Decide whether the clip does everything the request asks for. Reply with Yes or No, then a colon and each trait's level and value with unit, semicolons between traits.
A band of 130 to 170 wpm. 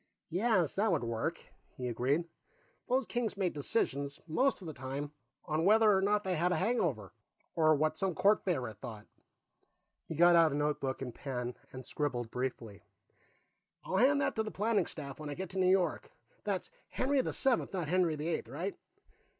No: average, 185 wpm